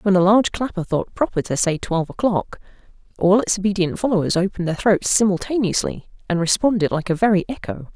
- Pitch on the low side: No, high, 195 Hz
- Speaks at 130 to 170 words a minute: No, average, 180 wpm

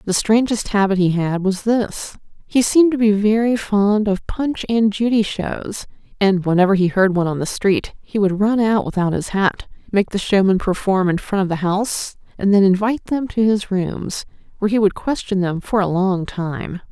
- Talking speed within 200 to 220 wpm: Yes, fast, 205 wpm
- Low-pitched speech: No, high, 200 Hz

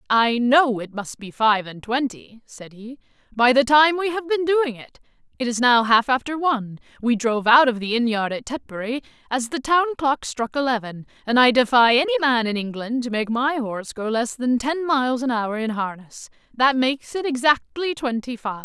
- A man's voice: No, female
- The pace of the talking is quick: Yes, fast, 210 wpm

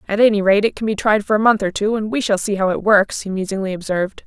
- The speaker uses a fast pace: Yes, fast, 310 wpm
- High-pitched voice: Yes, high, 205 Hz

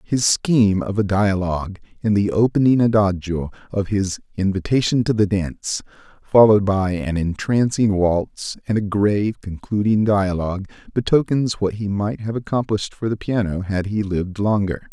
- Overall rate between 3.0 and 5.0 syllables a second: Yes, 4.9 syllables/s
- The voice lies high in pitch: No, low, 100 Hz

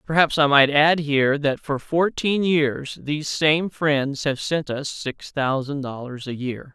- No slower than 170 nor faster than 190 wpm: Yes, average, 180 wpm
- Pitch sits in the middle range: Yes, medium, 145 Hz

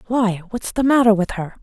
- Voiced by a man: No, female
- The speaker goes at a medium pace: No, fast, 220 wpm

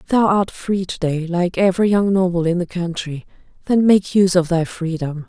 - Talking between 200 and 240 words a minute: Yes, fast, 205 wpm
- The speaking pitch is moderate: Yes, medium, 180 Hz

